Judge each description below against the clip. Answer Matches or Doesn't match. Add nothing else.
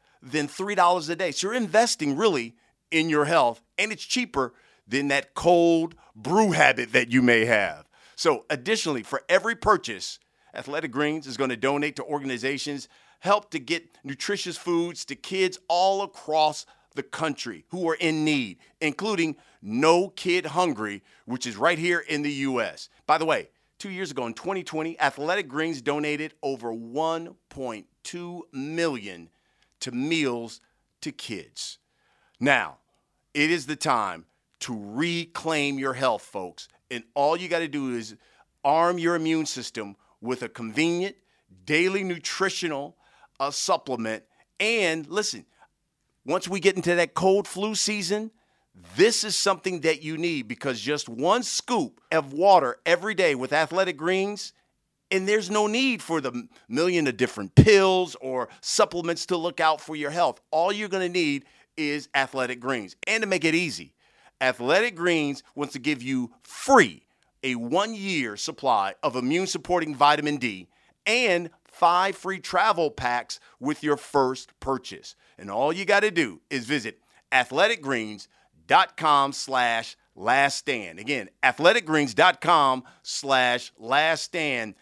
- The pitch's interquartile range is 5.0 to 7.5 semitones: Matches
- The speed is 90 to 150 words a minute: Matches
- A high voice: Doesn't match